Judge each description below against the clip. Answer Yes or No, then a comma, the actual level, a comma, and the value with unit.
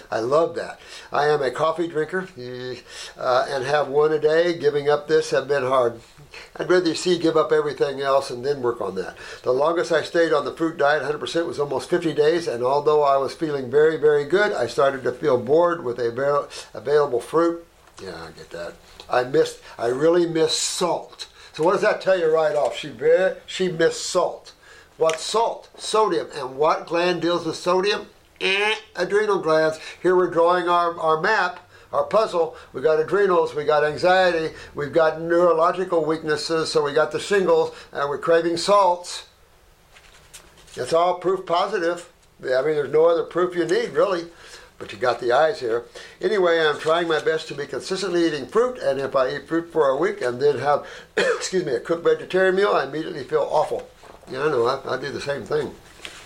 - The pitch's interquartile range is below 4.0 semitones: No, average, 4.6 semitones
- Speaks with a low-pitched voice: No, medium, 170 Hz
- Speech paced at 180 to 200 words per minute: Yes, average, 195 wpm